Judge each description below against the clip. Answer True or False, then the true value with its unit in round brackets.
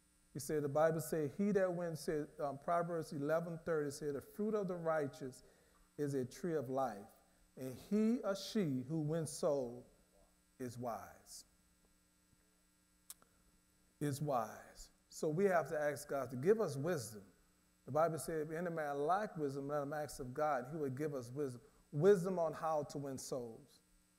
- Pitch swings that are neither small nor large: False (8.9 semitones)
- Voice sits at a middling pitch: True (145 Hz)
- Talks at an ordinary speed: True (170 wpm)